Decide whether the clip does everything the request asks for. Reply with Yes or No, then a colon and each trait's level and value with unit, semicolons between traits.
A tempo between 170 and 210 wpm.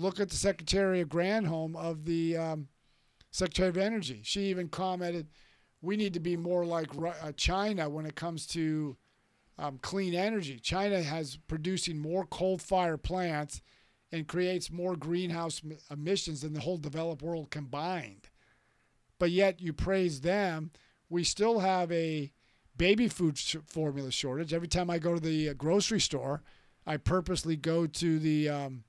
No: average, 160 wpm